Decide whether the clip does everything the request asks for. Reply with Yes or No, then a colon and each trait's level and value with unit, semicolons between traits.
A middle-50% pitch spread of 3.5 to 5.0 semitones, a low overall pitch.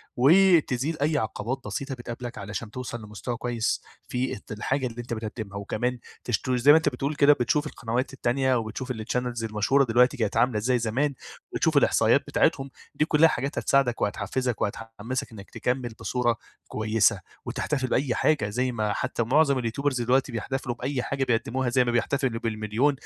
No: average, 3.0 semitones; low, 125 Hz